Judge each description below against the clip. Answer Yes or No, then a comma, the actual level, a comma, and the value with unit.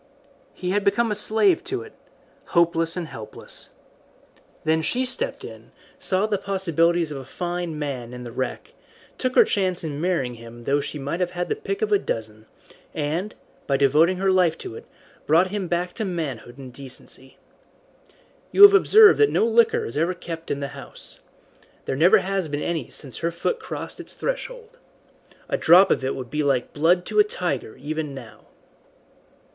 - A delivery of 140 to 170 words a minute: No, average, 185 wpm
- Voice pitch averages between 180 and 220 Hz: No, medium, 170 Hz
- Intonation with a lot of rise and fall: Yes, wide, 6.2 semitones